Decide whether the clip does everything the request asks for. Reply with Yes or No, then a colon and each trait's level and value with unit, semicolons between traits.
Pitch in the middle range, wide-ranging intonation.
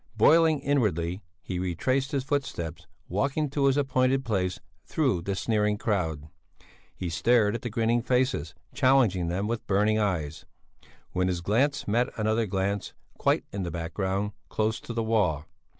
No: low, 105 Hz; wide, 5.8 semitones